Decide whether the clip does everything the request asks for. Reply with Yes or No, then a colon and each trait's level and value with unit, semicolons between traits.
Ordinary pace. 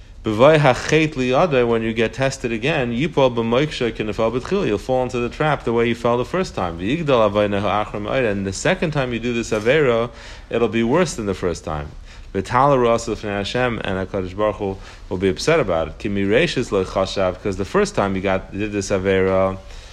Yes: average, 150 wpm